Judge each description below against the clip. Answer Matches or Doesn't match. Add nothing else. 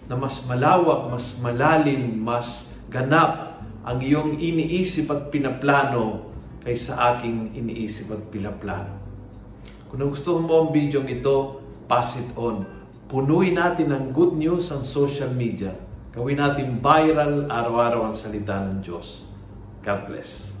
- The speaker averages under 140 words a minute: Matches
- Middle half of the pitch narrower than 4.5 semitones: Doesn't match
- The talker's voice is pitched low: Matches